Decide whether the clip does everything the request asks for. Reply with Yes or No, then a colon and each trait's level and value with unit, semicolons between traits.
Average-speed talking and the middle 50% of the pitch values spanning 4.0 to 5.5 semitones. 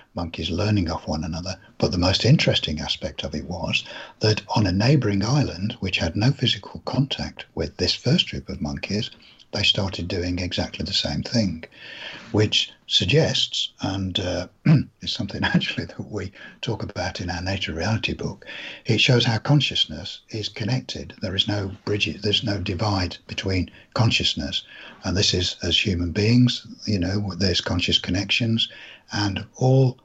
No: average, 160 wpm; average, 3.6 semitones